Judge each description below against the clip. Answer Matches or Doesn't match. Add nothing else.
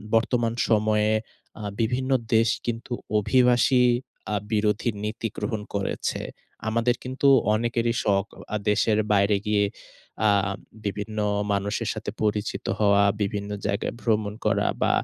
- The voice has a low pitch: Matches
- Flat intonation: Matches